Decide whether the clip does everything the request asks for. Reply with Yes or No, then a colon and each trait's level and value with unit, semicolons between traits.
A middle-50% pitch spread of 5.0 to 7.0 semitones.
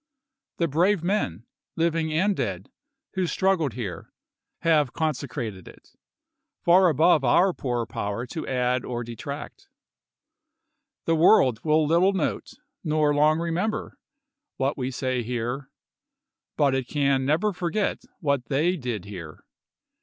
Yes: wide, 5.4 semitones